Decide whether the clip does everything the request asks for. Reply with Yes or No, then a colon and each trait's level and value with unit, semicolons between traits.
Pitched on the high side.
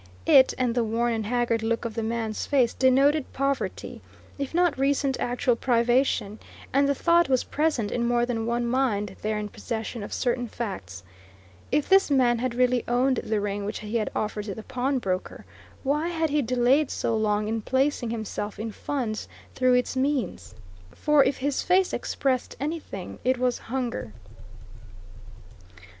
Yes: high, 245 Hz